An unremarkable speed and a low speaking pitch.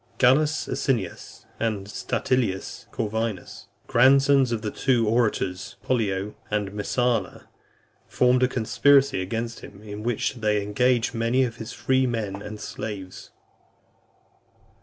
No: slow, 115 wpm; low, 115 Hz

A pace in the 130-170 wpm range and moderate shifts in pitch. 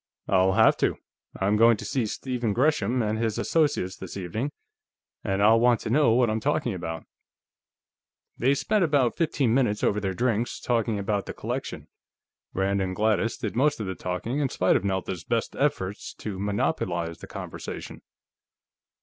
Yes: average, 165 wpm; average, 4.3 semitones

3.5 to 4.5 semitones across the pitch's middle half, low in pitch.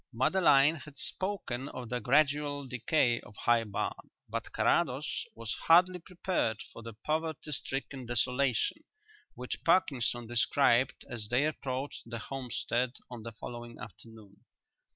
Yes: average, 3.9 semitones; low, 125 Hz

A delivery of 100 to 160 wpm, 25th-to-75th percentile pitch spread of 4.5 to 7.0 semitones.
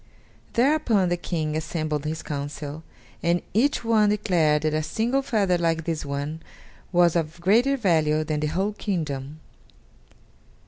Yes: average, 140 wpm; average, 5.1 semitones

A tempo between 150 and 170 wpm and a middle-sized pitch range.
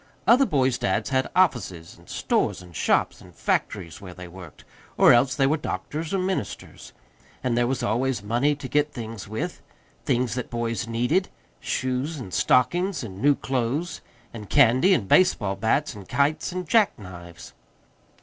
No: average, 165 wpm; wide, 5.8 semitones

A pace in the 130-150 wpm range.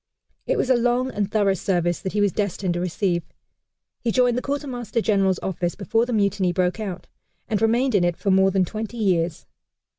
No: average, 200 wpm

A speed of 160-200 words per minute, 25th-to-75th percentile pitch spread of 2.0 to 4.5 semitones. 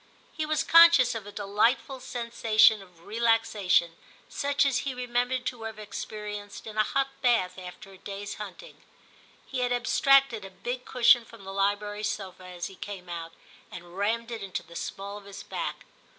Yes: average, 180 wpm; average, 3.9 semitones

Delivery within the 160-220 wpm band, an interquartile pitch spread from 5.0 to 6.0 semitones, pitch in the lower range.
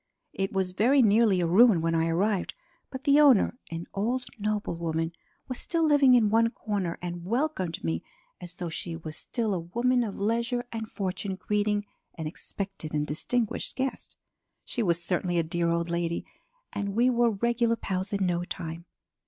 No: average, 175 wpm; wide, 5.5 semitones; high, 200 Hz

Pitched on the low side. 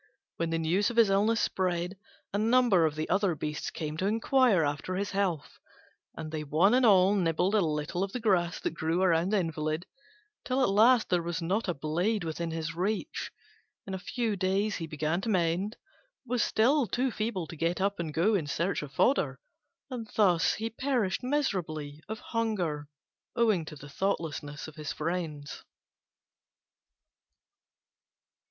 No: medium, 185 Hz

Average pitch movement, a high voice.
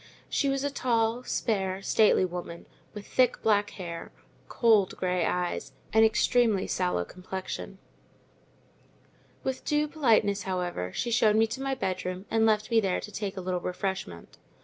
Yes: average, 3.8 semitones; high, 205 Hz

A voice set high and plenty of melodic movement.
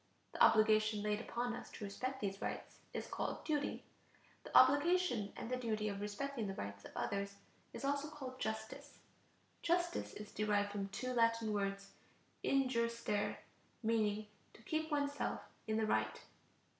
No: high, 220 Hz; average, 4.3 semitones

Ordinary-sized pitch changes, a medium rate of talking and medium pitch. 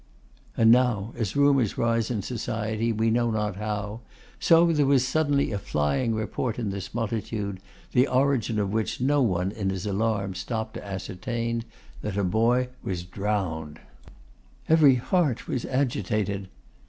No: average, 3.8 semitones; average, 150 wpm; low, 110 Hz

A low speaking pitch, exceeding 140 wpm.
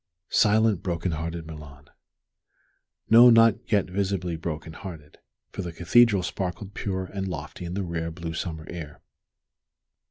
No: very low, 85 Hz; slow, 135 wpm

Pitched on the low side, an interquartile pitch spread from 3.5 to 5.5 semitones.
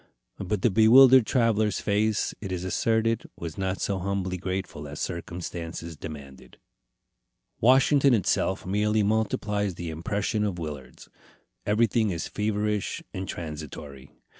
Yes: low, 100 Hz; average, 4.2 semitones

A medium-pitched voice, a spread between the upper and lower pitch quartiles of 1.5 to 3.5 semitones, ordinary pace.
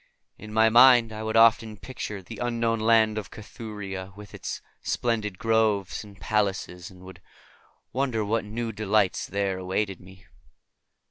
No: low, 105 Hz; narrow, 2.6 semitones; average, 145 wpm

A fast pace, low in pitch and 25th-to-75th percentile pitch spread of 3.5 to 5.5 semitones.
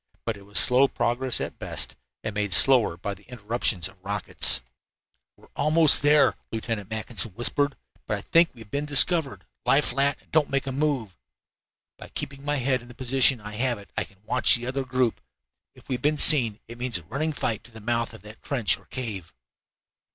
Yes: fast, 210 wpm; low, 120 Hz; average, 4.4 semitones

